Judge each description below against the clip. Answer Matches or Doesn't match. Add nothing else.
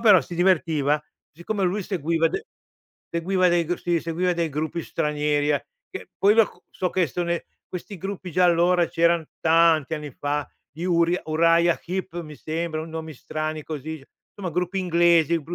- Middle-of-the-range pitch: Matches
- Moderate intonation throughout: Doesn't match